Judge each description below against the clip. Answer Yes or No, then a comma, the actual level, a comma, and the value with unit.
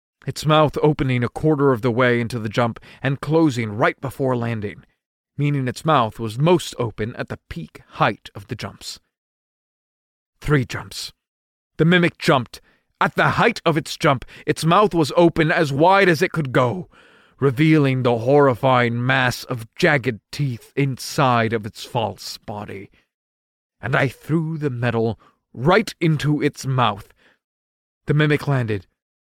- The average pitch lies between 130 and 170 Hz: Yes, low, 135 Hz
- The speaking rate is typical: Yes, average, 150 wpm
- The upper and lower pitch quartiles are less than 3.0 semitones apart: No, average, 4.7 semitones